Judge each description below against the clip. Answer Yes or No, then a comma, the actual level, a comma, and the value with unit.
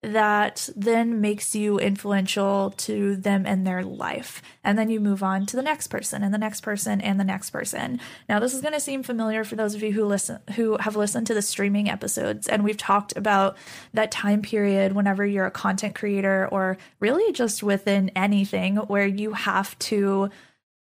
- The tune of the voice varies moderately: No, narrow, 1.6 semitones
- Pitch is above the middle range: Yes, high, 205 Hz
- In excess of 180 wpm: Yes, average, 195 wpm